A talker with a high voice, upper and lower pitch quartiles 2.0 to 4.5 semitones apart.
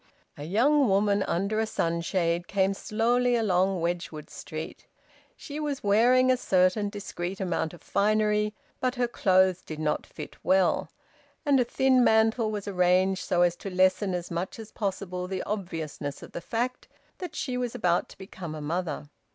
Yes: high, 195 Hz; average, 4.1 semitones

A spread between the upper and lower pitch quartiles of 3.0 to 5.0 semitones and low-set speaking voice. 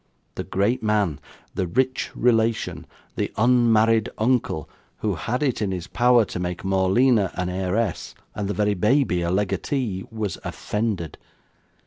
Yes: average, 3.9 semitones; low, 105 Hz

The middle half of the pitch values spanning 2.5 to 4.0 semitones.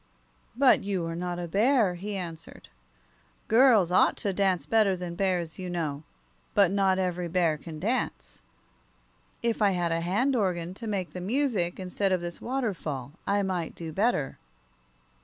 Yes: average, 3.1 semitones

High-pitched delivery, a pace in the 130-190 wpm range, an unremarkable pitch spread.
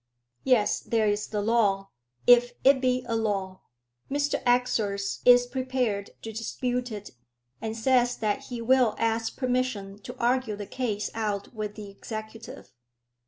Yes: high, 225 Hz; average, 145 wpm; average, 3.2 semitones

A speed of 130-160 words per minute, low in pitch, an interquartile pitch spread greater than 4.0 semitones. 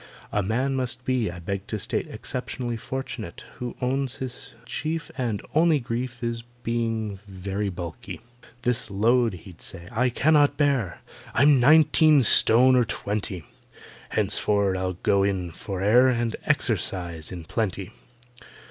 Yes: slow, 135 wpm; low, 115 Hz; average, 4.7 semitones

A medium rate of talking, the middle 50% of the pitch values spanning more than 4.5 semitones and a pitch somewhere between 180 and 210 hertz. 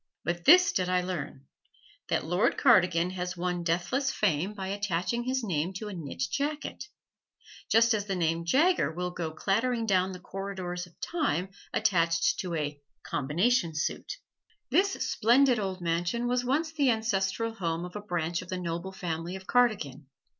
Yes: average, 165 wpm; average, 5.1 semitones; medium, 185 Hz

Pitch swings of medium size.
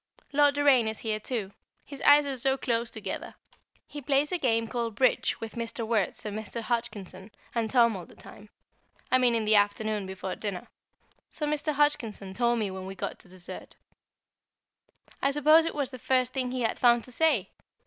Yes: average, 4.1 semitones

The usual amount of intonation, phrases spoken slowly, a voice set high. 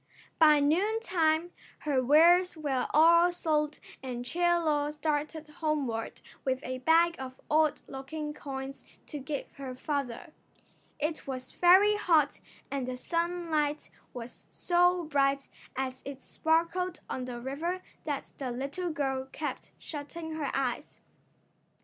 Yes: average, 3.8 semitones; slow, 130 wpm; very high, 300 Hz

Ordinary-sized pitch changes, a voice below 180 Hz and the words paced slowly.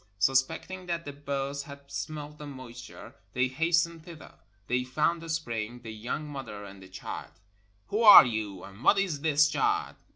No: average, 4.9 semitones; medium, 140 Hz; average, 175 wpm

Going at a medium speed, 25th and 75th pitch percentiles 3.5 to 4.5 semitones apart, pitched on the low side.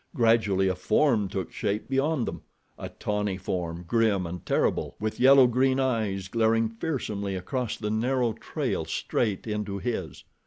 Yes: average, 145 wpm; average, 4.0 semitones; low, 110 Hz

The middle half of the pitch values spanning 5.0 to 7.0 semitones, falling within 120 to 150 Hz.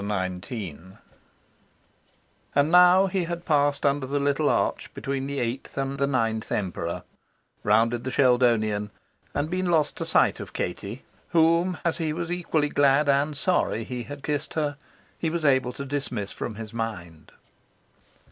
Yes: average, 5.3 semitones; medium, 140 Hz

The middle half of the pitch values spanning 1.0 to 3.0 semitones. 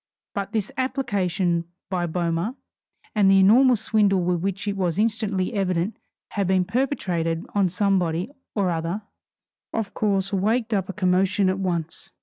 Yes: average, 2.7 semitones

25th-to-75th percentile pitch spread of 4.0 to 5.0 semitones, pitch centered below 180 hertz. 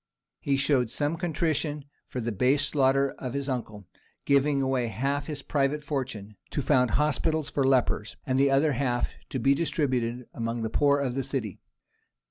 No: narrow, 2.6 semitones; low, 135 Hz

